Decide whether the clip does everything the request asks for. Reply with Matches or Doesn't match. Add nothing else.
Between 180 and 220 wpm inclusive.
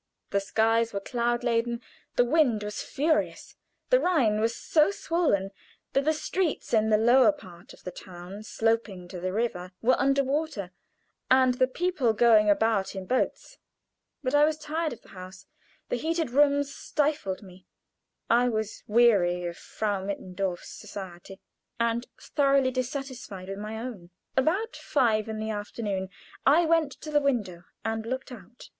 Doesn't match